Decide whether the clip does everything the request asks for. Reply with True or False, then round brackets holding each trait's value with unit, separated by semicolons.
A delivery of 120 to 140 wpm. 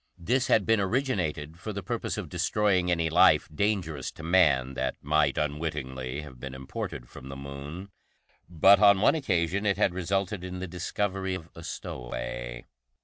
False (165 wpm)